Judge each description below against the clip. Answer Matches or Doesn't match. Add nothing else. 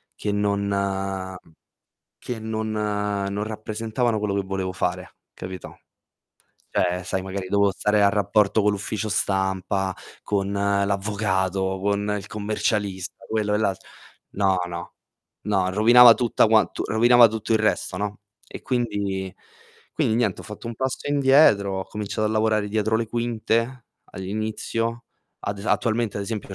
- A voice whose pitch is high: Doesn't match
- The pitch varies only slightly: Matches